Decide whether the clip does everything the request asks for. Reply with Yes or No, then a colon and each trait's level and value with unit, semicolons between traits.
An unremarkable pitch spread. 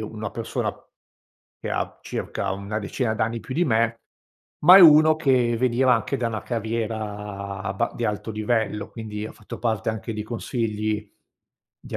No: narrow, 2.2 semitones